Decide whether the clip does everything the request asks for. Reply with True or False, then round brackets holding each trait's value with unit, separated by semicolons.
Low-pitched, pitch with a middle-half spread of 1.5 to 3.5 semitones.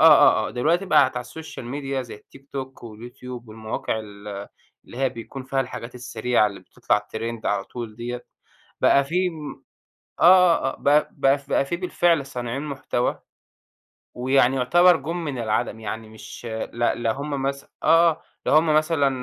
False (130 Hz; 4.3 semitones)